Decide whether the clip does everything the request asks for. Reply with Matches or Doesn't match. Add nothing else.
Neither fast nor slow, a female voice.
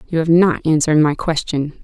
Matches